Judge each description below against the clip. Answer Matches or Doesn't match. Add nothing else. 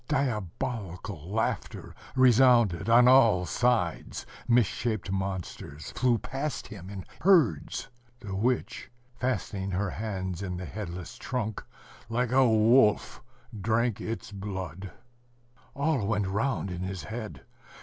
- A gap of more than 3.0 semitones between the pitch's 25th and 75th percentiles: Matches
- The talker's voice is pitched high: Doesn't match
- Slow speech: Matches